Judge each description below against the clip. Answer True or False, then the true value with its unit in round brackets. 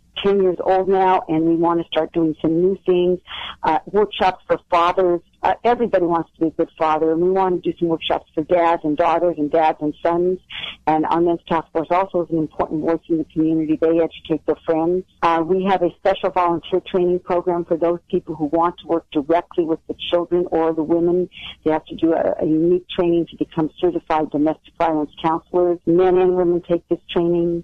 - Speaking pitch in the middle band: True (170 Hz)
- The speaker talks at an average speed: False (215 wpm)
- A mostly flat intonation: True (1.7 semitones)